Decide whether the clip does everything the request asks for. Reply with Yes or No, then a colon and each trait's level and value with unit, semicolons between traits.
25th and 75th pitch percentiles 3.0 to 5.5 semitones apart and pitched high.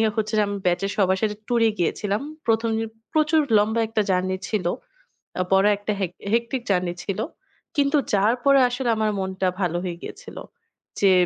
Yes: average, 3.5 semitones; high, 210 Hz